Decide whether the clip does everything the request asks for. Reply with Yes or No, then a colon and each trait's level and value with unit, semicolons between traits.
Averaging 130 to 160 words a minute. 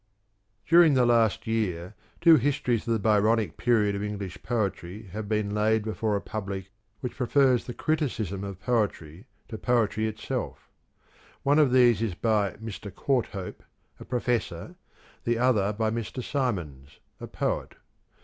Yes: average, 145 wpm